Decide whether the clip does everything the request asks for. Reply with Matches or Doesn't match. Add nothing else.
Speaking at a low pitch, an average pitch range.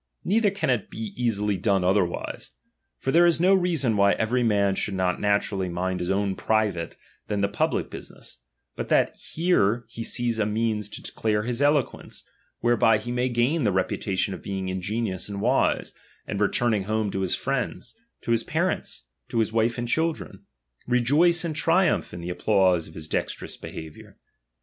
Matches